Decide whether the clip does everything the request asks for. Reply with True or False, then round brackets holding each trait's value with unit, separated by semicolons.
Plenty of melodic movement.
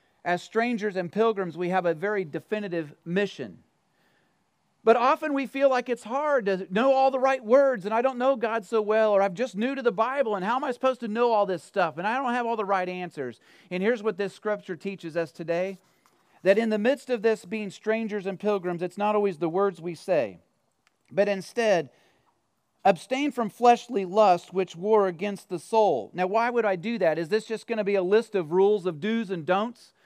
False (3.8 semitones)